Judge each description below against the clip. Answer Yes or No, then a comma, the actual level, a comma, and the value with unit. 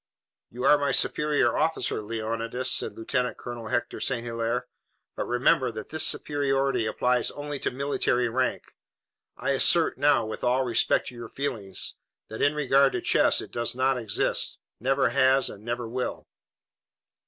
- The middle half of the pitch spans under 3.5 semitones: Yes, average, 2.9 semitones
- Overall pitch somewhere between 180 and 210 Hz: No, low, 125 Hz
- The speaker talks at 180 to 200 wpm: No, average, 155 wpm